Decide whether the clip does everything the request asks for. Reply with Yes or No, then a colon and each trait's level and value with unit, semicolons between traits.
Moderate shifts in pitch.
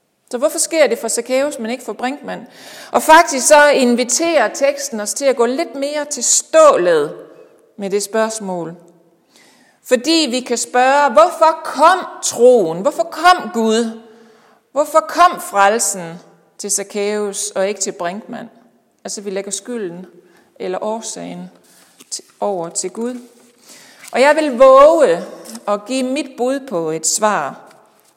No: wide, 6.0 semitones